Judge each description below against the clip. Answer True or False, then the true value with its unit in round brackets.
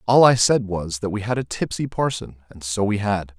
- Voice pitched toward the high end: False (105 Hz)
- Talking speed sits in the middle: False (230 wpm)